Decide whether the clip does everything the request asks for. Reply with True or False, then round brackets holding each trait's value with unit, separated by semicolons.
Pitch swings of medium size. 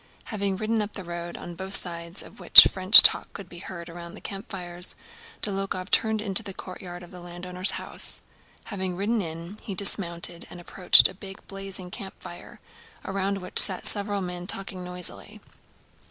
False (2.0 semitones)